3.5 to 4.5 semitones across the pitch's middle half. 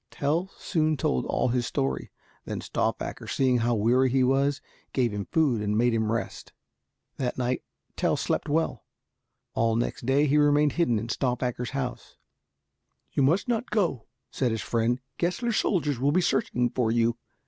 Yes: average, 3.9 semitones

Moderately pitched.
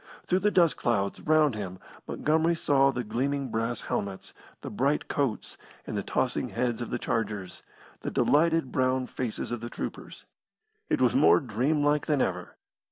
No: low, 130 Hz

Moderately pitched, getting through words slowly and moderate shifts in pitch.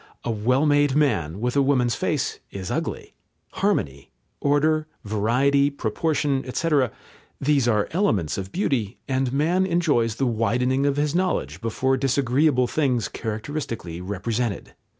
No: low, 130 Hz; slow, 130 wpm; average, 4.5 semitones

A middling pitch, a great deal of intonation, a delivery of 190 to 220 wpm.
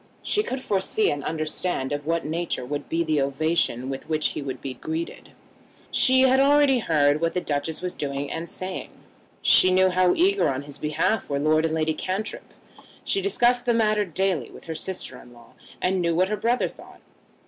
Yes: medium, 165 Hz; wide, 5.7 semitones; average, 195 wpm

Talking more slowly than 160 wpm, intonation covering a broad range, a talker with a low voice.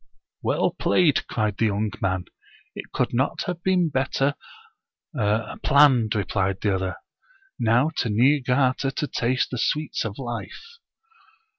No: average, 145 wpm; average, 5.0 semitones; low, 125 Hz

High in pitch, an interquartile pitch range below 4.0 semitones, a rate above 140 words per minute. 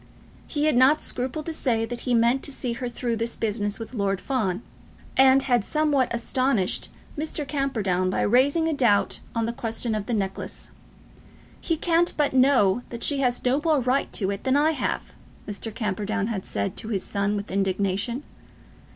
No: high, 240 Hz; average, 4.8 semitones; average, 185 wpm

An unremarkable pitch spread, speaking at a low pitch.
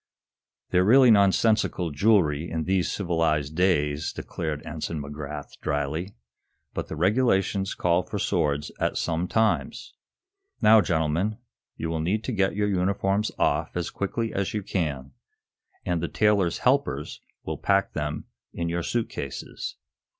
Yes: average, 4.7 semitones; very low, 90 Hz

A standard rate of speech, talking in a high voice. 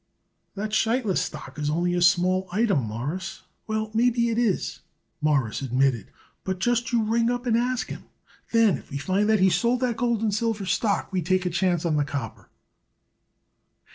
Yes: average, 180 wpm; high, 195 Hz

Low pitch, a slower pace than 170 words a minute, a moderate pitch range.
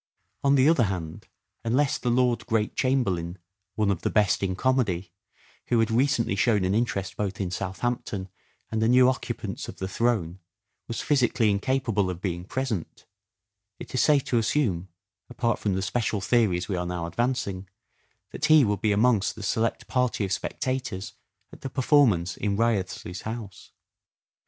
No: low, 110 Hz; average, 175 wpm; average, 4.7 semitones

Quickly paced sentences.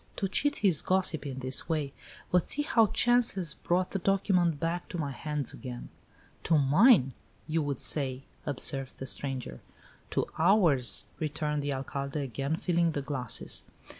No: average, 160 wpm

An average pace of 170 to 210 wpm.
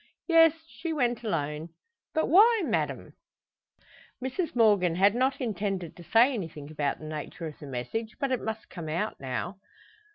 No: average, 160 wpm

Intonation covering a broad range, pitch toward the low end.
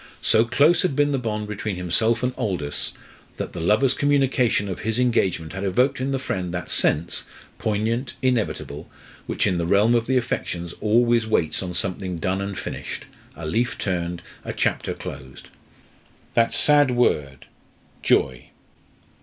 Yes: wide, 5.9 semitones; low, 105 Hz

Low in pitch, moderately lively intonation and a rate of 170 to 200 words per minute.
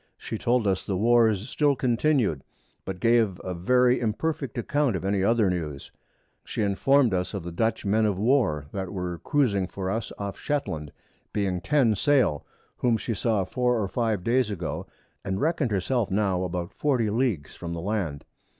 Yes: low, 105 Hz; average, 4.8 semitones; average, 175 wpm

